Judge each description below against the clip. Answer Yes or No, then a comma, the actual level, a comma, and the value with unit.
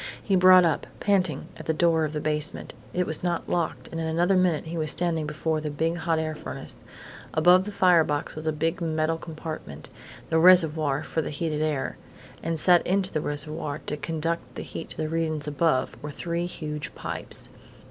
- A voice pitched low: No, medium, 160 Hz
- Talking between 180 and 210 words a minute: Yes, average, 200 wpm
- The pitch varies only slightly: Yes, narrow, 2.0 semitones